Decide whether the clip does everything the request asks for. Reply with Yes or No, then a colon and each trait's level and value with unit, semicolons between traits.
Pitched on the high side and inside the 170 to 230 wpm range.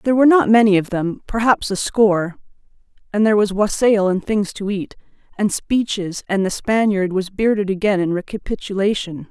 No: high, 205 Hz; average, 160 wpm